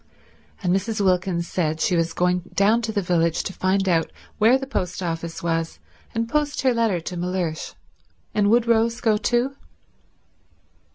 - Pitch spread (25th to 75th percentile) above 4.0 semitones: Yes, average, 4.9 semitones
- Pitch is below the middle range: No, high, 190 Hz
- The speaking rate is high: No, average, 165 wpm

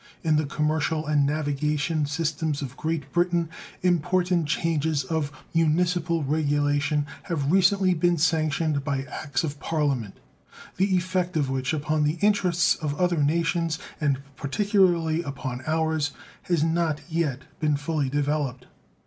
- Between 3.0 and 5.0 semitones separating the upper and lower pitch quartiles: No, narrow, 2.6 semitones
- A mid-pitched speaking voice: Yes, medium, 155 Hz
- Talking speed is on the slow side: Yes, slow, 130 wpm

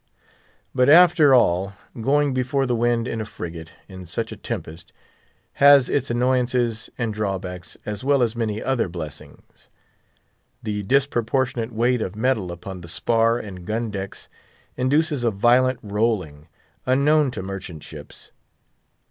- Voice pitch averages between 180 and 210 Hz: No, low, 115 Hz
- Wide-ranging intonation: No, average, 4.8 semitones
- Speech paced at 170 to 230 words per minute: No, average, 140 wpm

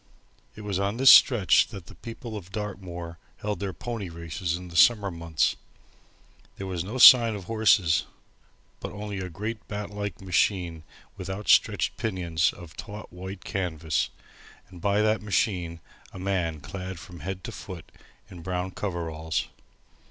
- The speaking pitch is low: Yes, very low, 95 Hz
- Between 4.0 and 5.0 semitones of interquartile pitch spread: No, average, 3.4 semitones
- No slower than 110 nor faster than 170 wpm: Yes, average, 160 wpm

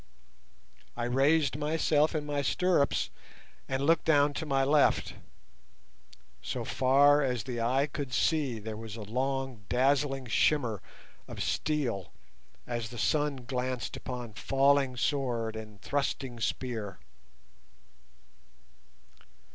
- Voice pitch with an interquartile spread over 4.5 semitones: No, average, 3.2 semitones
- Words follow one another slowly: Yes, slow, 115 wpm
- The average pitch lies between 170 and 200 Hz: No, low, 135 Hz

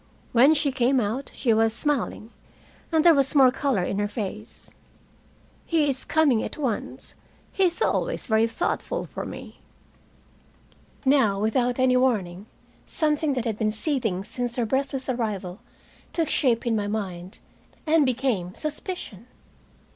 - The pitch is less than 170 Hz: No, very high, 250 Hz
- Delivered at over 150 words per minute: No, average, 145 wpm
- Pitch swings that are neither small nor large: Yes, average, 4.7 semitones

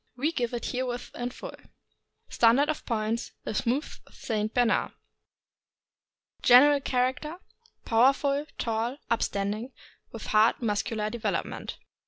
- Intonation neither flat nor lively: Yes, average, 3.1 semitones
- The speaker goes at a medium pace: No, slow, 120 wpm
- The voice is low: No, high, 240 Hz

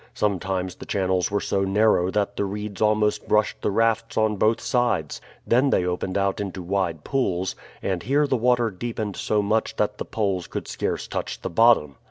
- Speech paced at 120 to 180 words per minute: No, average, 190 wpm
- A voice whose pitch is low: Yes, low, 105 Hz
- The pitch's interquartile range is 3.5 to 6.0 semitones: No, average, 3.0 semitones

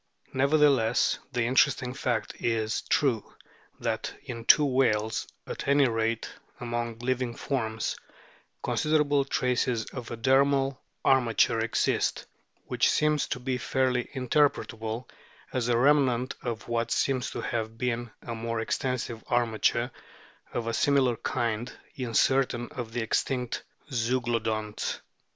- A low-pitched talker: Yes, low, 120 Hz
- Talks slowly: Yes, slow, 125 wpm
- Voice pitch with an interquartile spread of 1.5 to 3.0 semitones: Yes, narrow, 2.5 semitones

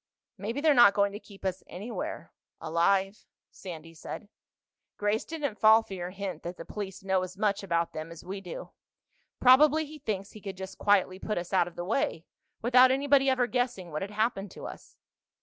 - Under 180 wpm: No, average, 190 wpm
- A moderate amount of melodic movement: Yes, average, 4.4 semitones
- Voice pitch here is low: No, high, 200 Hz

